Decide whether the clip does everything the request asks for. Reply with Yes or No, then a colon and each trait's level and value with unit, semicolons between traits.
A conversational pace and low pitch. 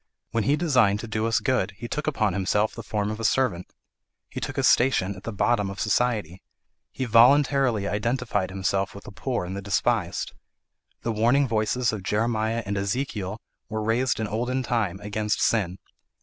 Yes: average, 180 wpm; low, 110 Hz